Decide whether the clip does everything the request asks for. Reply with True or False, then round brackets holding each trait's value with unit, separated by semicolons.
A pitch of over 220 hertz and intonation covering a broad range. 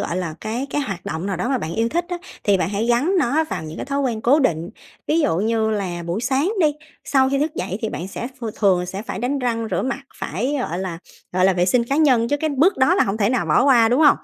True (230 Hz; 6.3 semitones)